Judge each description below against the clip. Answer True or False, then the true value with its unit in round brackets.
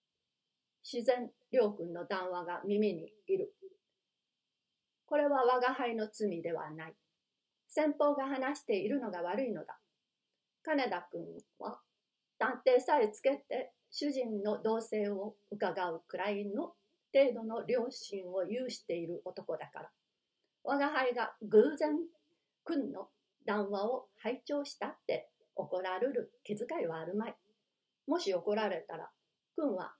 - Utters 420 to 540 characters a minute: False (240 characters per minute)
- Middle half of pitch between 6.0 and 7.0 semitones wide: False (5.4 semitones)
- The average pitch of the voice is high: True (225 Hz)